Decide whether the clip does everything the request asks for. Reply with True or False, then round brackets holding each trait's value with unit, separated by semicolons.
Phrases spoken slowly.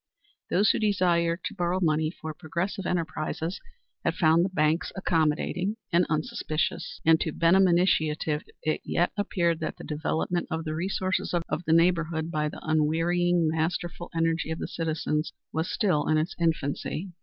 False (155 wpm)